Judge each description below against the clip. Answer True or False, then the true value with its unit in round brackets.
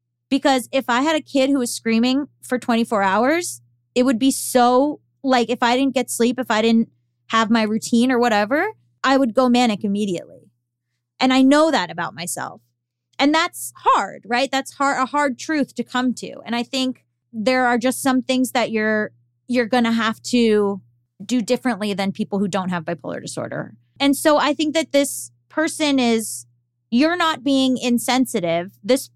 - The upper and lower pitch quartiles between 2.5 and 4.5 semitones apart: False (4.9 semitones)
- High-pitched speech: True (240 Hz)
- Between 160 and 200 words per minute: True (185 wpm)